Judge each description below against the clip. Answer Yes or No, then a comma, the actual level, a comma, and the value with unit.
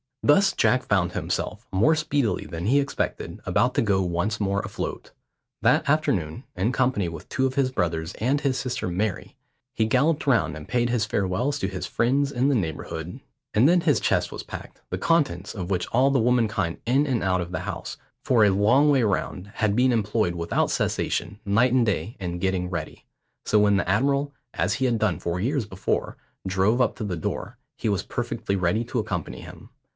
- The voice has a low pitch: Yes, low, 110 Hz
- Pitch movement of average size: No, wide, 5.8 semitones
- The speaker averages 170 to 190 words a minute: No, average, 200 wpm